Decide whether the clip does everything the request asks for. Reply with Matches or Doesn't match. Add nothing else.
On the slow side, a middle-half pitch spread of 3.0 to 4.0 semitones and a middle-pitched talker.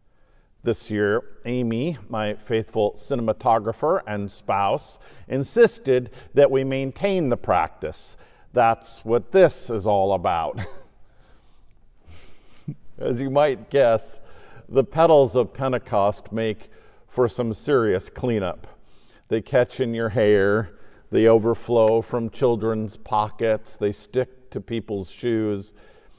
Doesn't match